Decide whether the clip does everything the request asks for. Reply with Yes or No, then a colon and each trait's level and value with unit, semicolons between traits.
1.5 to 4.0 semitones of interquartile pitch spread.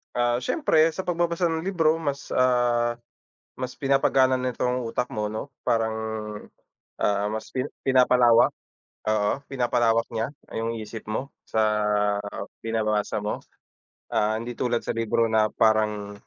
Yes: average, 3.0 semitones